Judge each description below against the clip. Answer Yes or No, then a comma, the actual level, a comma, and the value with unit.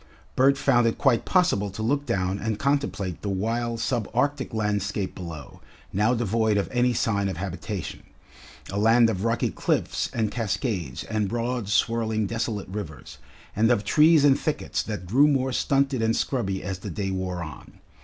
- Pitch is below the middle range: Yes, low, 110 Hz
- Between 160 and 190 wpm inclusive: Yes, average, 170 wpm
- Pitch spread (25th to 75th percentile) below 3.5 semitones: No, average, 3.9 semitones